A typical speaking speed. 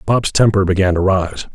Yes: average, 195 wpm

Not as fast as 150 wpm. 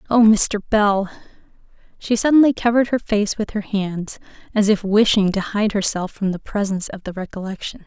No: average, 175 wpm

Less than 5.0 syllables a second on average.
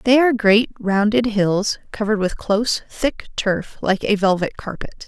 Yes: 4.5 syllables/s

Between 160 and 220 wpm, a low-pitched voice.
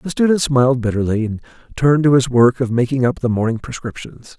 Yes: fast, 205 wpm; low, 130 Hz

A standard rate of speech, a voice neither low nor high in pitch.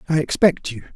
Yes: average, 190 wpm; medium, 155 Hz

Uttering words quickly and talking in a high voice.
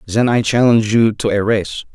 No: fast, 215 wpm; low, 110 Hz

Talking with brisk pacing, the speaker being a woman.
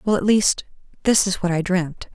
Yes: fast, 225 wpm; female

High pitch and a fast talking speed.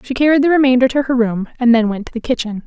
Yes: very high, 250 Hz; fast, 295 wpm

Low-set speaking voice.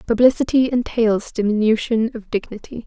No: high, 225 Hz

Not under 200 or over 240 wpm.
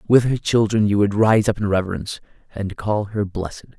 Yes: fast, 205 wpm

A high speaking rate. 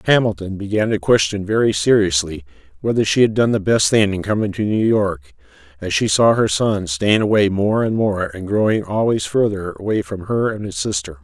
Yes: fast, 210 wpm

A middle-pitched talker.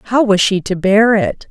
No: high, 205 Hz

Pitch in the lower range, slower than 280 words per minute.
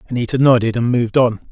Yes: low, 120 Hz; average, 200 wpm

